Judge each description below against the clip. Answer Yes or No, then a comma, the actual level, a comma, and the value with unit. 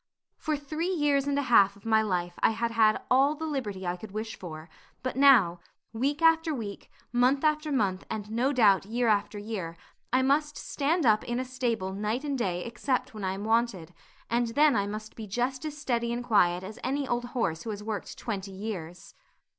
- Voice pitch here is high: Yes, high, 230 Hz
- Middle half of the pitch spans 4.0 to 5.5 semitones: Yes, average, 5.1 semitones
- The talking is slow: No, fast, 205 wpm